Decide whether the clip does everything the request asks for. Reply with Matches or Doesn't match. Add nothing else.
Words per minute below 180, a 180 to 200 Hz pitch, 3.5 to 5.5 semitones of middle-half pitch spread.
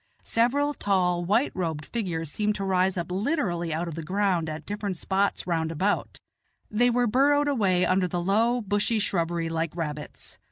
Matches